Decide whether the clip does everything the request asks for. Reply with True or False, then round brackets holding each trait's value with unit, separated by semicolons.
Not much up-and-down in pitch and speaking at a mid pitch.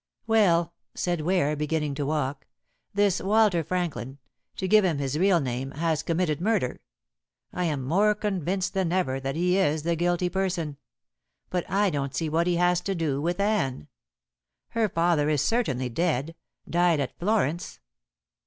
False (4.1 semitones; 170 Hz)